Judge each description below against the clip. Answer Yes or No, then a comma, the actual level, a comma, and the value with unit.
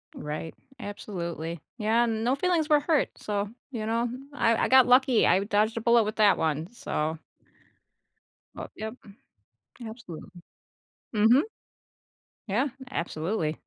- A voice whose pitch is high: Yes, high, 220 Hz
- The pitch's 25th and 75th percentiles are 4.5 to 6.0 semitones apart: Yes, average, 5.2 semitones